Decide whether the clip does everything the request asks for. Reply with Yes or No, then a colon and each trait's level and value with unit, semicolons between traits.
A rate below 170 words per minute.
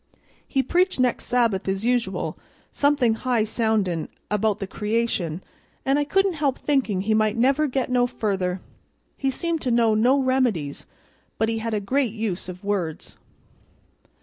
Yes: average, 155 wpm